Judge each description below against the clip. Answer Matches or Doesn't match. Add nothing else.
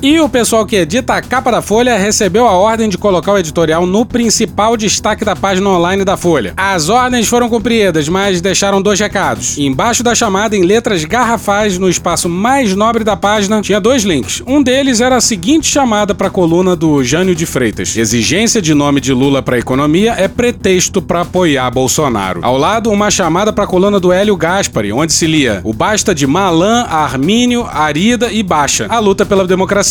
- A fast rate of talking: Matches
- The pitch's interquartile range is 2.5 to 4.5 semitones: Doesn't match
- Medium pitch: Doesn't match